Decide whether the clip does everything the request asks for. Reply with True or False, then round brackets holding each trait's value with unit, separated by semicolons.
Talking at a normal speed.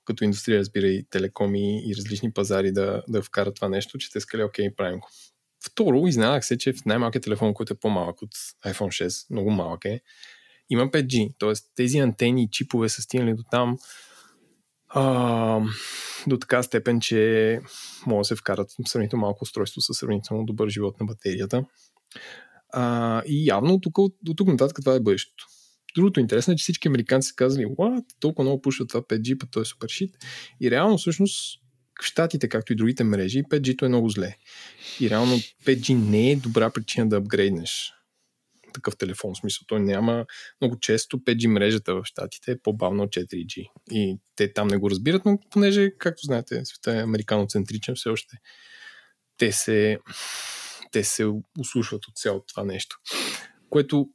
False (175 wpm)